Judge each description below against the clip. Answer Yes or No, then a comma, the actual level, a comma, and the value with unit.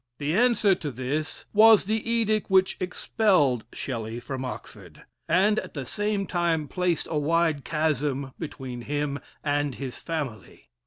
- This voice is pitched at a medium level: Yes, medium, 155 Hz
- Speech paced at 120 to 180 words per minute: Yes, average, 145 wpm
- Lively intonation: Yes, wide, 5.7 semitones